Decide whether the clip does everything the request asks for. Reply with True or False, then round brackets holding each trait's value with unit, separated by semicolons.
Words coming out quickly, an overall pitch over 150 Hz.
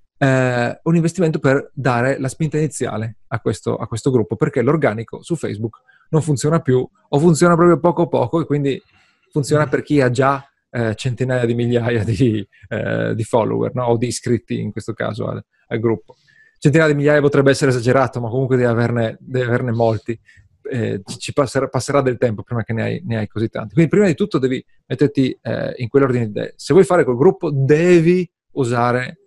False (190 wpm; 130 Hz)